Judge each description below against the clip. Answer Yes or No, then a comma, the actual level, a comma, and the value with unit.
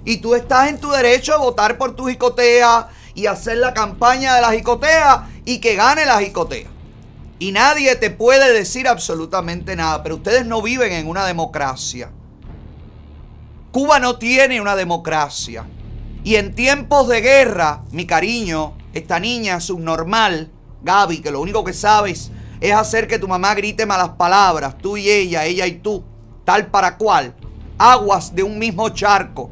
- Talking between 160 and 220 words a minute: Yes, average, 165 wpm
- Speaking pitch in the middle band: No, high, 205 Hz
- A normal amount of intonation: No, wide, 6.9 semitones